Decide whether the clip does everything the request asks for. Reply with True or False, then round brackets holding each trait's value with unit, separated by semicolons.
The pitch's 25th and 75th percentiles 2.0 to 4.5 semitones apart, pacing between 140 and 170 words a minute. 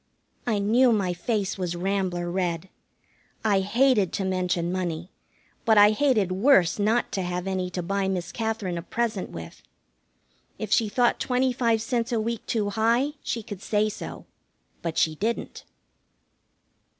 True (4.0 semitones; 155 wpm)